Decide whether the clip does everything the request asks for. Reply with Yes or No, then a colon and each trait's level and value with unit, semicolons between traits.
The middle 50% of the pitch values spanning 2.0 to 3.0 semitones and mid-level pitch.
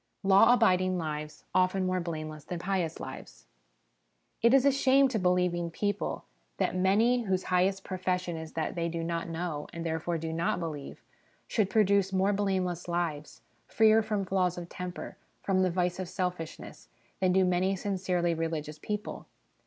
Yes: narrow, 2.5 semitones; medium, 180 Hz